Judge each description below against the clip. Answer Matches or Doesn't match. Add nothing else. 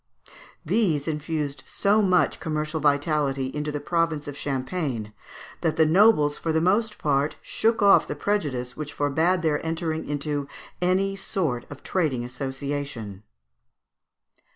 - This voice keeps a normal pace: Doesn't match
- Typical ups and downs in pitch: Matches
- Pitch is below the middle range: Doesn't match